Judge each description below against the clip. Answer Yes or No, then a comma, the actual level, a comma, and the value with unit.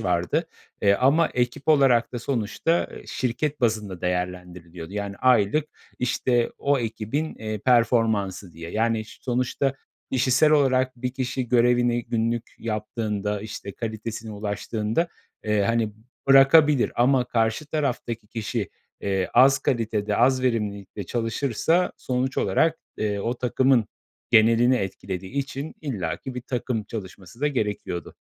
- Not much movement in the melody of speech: No, average, 3.8 semitones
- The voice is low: Yes, low, 115 Hz